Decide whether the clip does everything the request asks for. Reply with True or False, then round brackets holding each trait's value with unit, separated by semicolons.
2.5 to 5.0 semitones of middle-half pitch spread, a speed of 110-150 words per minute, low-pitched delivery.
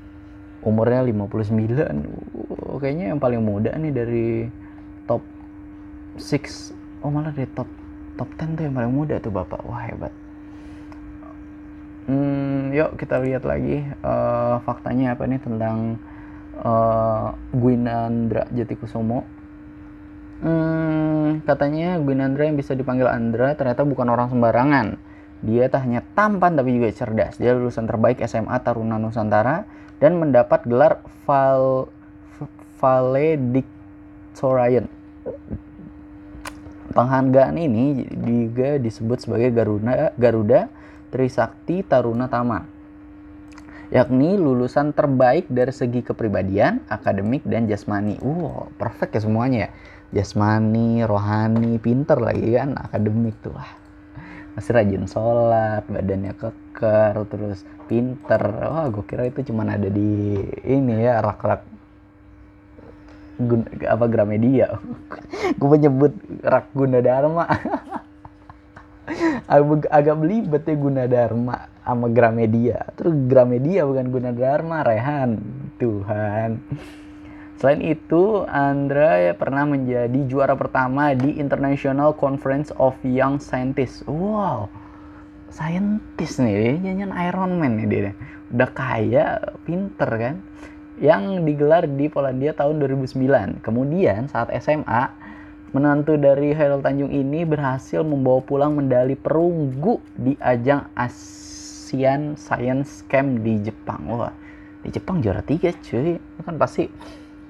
False (5.4 semitones; 115 wpm; 120 Hz)